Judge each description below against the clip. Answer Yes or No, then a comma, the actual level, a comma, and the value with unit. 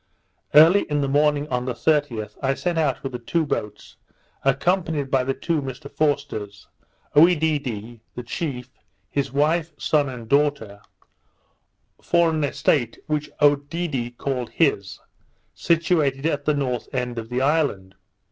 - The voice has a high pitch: No, medium, 140 Hz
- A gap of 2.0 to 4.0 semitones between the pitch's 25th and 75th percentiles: Yes, average, 3.7 semitones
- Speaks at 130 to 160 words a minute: Yes, average, 140 wpm